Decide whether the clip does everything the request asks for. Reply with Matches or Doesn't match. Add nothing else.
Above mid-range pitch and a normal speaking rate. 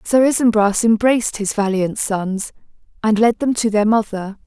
Matches